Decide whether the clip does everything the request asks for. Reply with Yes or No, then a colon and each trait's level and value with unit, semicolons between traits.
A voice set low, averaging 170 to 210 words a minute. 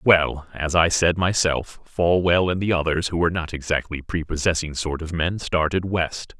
Yes: very low, 85 Hz; average, 180 wpm